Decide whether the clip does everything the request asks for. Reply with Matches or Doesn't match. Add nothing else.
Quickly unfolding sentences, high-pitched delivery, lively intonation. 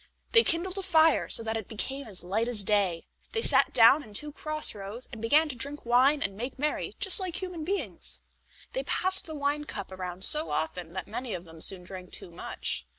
Matches